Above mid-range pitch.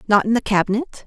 Yes: high, 220 Hz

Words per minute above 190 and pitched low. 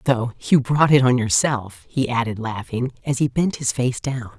Yes: fast, 205 wpm; low, 125 Hz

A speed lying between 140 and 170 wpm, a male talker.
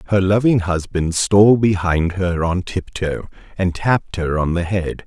Yes: average, 165 wpm; male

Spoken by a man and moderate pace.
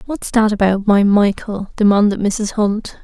No: female; average, 160 wpm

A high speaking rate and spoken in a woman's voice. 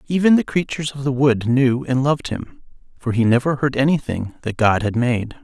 No: fast, 210 wpm; male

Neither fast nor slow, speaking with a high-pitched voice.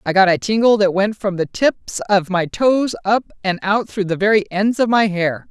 No: fast, 240 wpm; high, 200 Hz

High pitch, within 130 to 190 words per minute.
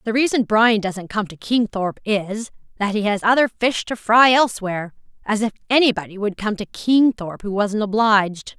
Yes: high, 215 Hz; average, 180 wpm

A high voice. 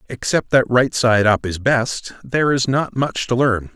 No: low, 120 Hz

